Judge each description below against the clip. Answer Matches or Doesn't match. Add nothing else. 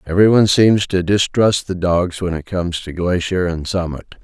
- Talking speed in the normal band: Matches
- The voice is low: Matches